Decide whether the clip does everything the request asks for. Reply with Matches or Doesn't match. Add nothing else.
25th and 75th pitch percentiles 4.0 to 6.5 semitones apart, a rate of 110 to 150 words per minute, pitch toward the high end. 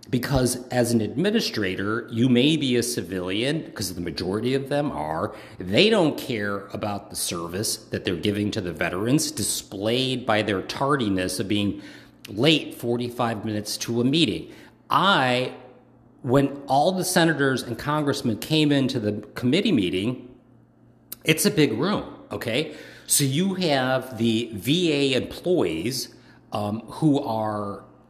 Doesn't match